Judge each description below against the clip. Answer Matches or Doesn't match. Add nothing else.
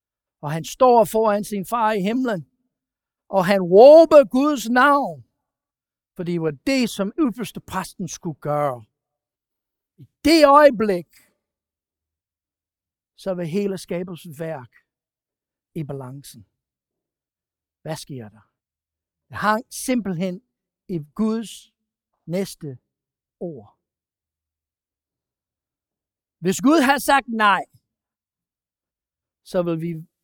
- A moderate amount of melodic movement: Doesn't match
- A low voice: Doesn't match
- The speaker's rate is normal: Doesn't match